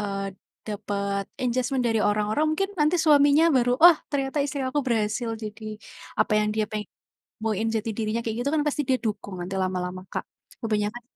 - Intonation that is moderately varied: Yes, average, 4.4 semitones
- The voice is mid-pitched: No, high, 225 Hz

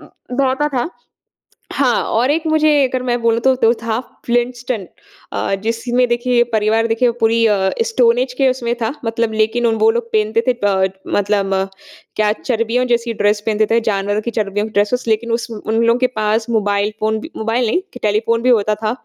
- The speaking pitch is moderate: No, high, 230 Hz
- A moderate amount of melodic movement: No, narrow, 2.2 semitones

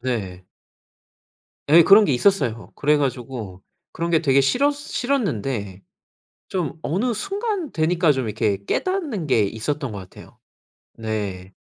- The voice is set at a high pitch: No, medium, 140 Hz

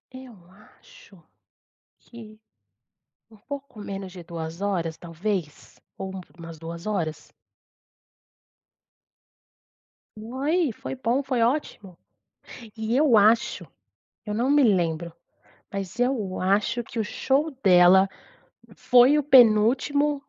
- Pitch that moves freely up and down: Yes, wide, 5.9 semitones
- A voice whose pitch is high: Yes, high, 215 Hz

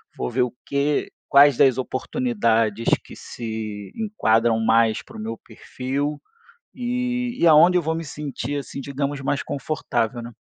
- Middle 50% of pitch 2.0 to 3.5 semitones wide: No, average, 5.1 semitones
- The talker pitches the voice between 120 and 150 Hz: Yes, medium, 140 Hz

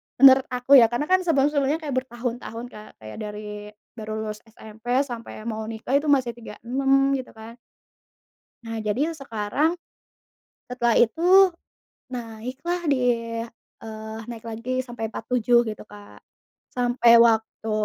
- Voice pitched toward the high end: Yes, high, 240 Hz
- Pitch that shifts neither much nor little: Yes, average, 3.3 semitones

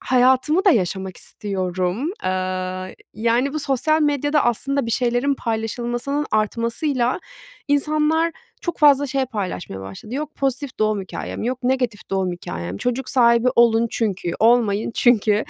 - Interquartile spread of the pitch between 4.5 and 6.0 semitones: Yes, average, 5.2 semitones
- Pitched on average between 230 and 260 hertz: Yes, high, 240 Hz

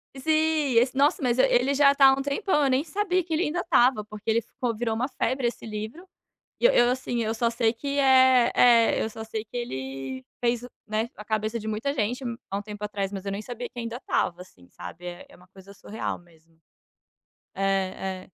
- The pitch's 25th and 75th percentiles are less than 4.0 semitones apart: No, average, 4.5 semitones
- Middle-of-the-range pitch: No, high, 235 Hz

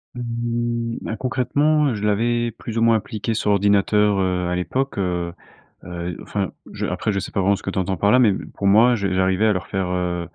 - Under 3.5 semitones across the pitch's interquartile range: No, average, 3.8 semitones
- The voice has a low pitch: Yes, low, 105 Hz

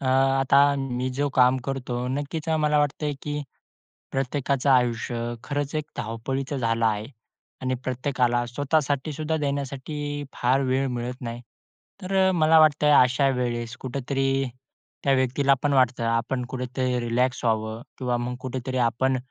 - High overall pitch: No, low, 130 Hz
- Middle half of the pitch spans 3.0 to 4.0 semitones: No, narrow, 2.6 semitones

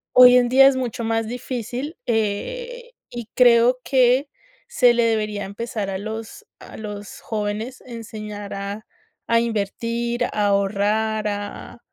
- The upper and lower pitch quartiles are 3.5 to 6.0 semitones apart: No, average, 2.9 semitones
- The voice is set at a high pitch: Yes, high, 230 Hz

